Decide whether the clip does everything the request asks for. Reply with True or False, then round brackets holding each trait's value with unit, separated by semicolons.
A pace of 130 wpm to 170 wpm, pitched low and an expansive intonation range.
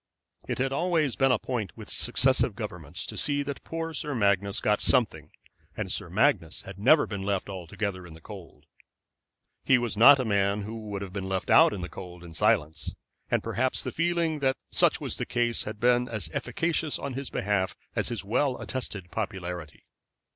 False (190 wpm; 110 Hz; 5.7 semitones)